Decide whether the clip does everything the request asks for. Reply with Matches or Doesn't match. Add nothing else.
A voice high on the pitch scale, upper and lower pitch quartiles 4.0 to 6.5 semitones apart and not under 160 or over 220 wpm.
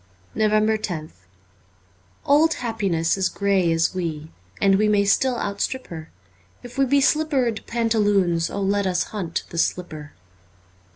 Doesn't match